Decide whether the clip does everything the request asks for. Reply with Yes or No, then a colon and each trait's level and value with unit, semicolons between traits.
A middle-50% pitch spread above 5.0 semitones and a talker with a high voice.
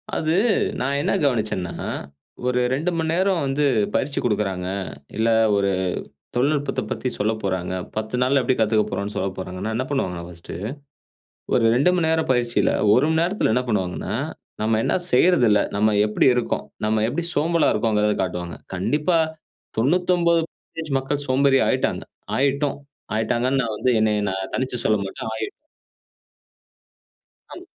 No: wide, 5.4 semitones; low, 125 Hz